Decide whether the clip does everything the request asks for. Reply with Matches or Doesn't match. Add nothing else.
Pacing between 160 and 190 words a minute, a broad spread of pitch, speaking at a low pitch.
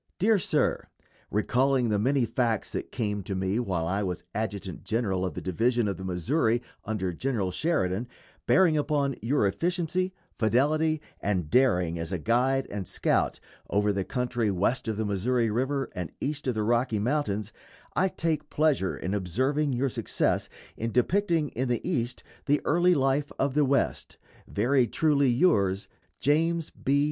Matches